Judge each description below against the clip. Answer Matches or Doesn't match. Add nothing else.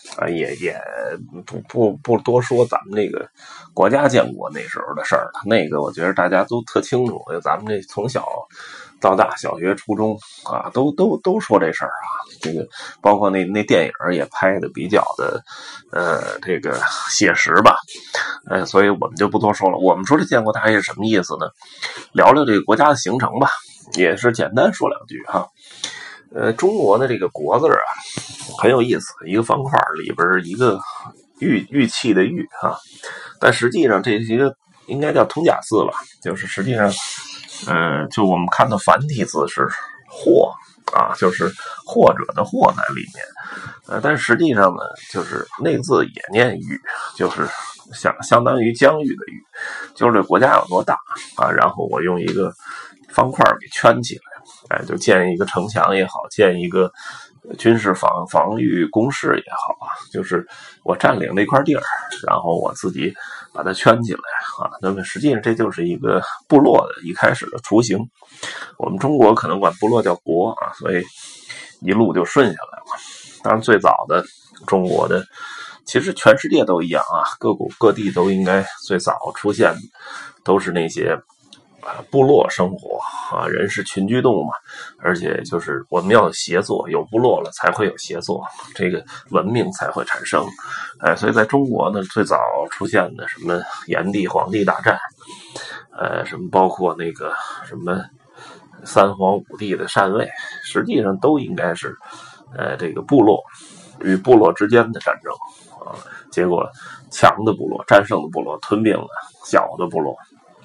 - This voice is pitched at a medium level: Doesn't match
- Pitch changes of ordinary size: Matches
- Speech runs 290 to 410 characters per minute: Doesn't match